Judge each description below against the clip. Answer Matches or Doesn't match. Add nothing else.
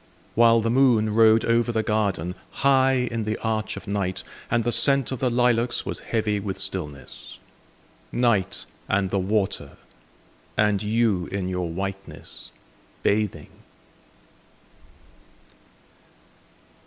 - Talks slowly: Matches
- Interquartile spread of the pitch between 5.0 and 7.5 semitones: Doesn't match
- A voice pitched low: Matches